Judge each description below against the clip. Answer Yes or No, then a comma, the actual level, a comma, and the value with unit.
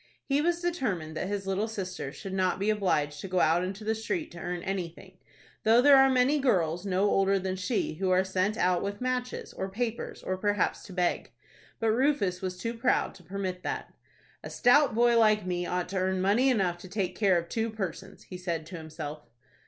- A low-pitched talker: No, high, 195 Hz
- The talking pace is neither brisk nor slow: No, fast, 210 wpm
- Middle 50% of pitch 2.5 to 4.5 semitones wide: Yes, average, 3.8 semitones